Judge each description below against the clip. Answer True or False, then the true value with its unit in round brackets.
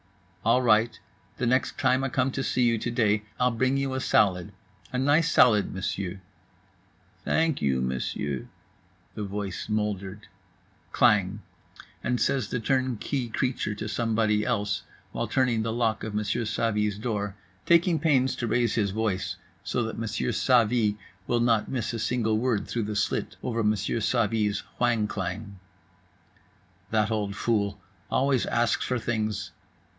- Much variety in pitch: False (3.1 semitones)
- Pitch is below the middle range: True (110 Hz)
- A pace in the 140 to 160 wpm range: True (150 wpm)